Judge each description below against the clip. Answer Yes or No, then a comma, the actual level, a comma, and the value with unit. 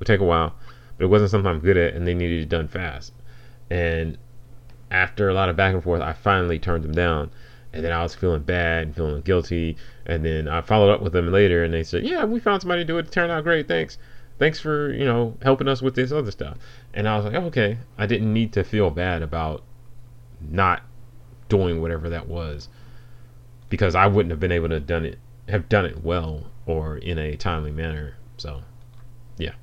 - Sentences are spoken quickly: Yes, fast, 225 wpm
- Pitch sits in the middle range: No, low, 100 Hz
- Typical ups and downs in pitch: No, wide, 6.2 semitones